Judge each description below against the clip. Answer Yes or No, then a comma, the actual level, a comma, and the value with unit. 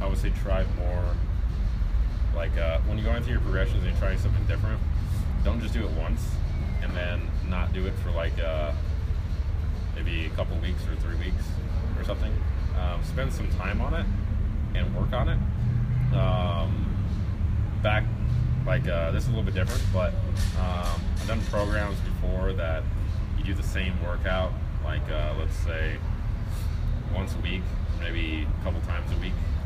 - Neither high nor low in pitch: No, very low, 90 Hz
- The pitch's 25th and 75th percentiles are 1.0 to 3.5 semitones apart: Yes, average, 2.8 semitones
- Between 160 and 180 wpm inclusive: Yes, average, 175 wpm